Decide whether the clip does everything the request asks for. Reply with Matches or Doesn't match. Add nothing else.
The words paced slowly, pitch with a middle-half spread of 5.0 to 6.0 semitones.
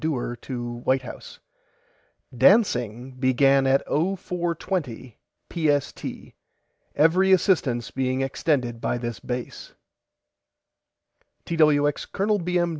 Matches